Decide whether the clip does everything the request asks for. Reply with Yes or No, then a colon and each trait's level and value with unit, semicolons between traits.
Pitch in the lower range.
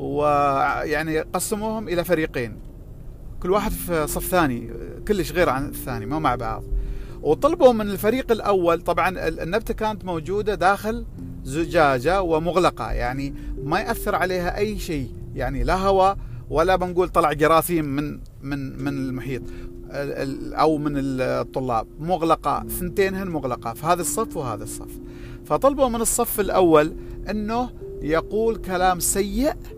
No: medium, 165 Hz